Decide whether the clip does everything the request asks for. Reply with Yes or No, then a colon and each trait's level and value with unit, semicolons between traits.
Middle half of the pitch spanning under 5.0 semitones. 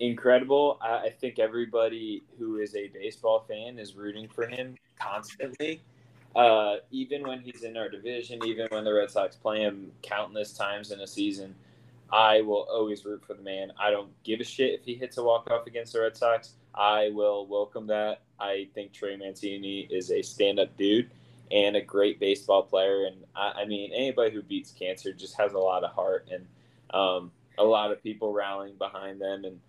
Yes: average, 3.9 semitones